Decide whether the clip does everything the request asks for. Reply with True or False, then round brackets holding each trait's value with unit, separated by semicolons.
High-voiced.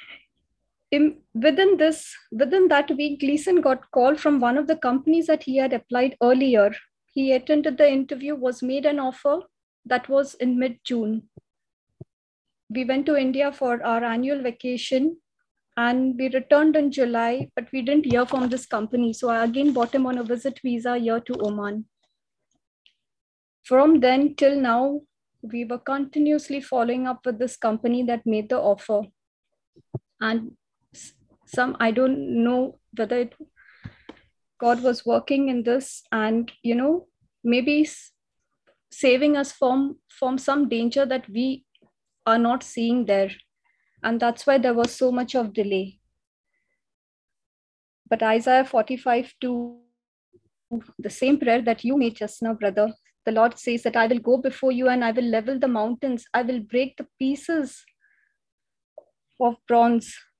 True (255 Hz)